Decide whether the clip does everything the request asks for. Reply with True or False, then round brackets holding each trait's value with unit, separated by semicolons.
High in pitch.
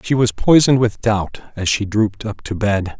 False (110 Hz)